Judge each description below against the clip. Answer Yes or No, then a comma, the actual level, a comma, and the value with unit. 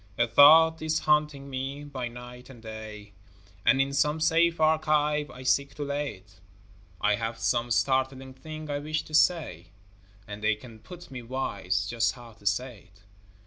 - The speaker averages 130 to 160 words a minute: No, average, 175 wpm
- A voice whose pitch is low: Yes, low, 130 Hz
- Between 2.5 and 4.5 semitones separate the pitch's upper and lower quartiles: No, average, 4.9 semitones